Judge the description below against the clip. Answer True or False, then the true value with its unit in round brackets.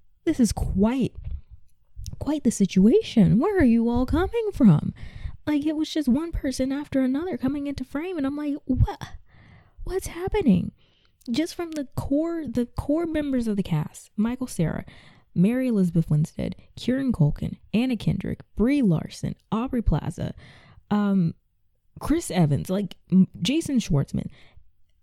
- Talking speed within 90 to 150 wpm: True (140 wpm)